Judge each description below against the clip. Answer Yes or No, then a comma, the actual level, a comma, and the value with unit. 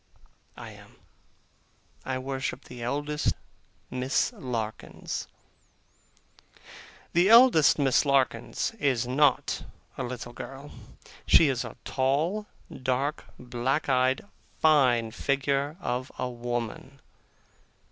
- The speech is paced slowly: Yes, slow, 95 wpm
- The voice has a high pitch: No, low, 130 Hz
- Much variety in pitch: No, narrow, 2.6 semitones